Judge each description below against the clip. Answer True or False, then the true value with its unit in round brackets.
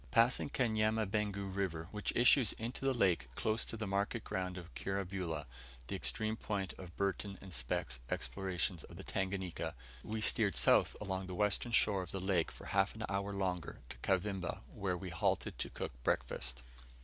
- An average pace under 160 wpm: False (175 wpm)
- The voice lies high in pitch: False (95 Hz)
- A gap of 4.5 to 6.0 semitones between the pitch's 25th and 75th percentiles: False (2.8 semitones)